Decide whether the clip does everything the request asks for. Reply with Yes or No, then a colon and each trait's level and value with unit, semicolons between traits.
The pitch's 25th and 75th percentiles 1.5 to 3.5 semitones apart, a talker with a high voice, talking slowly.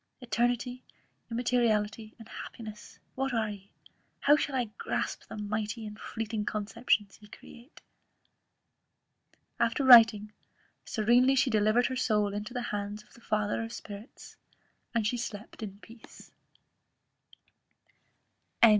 Yes: narrow, 2.5 semitones; high, 225 Hz; slow, 120 wpm